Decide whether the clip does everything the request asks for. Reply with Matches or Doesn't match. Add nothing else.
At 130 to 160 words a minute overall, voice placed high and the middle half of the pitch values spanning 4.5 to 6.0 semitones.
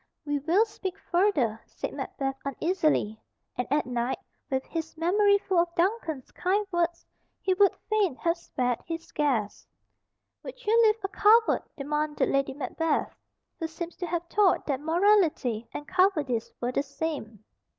Matches